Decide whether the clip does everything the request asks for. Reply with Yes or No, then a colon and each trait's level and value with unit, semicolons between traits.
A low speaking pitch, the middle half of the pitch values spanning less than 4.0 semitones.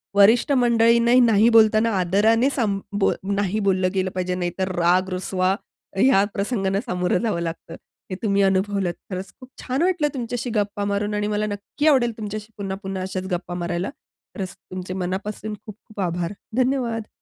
No: high, 200 Hz; average, 3.5 semitones